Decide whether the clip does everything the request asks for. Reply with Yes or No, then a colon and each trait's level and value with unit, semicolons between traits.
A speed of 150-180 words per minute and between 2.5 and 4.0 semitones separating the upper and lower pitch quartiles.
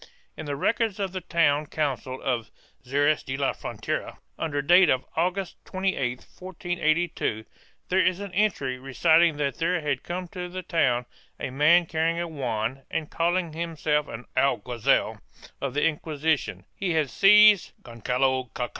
No: average, 155 wpm; average, 4.9 semitones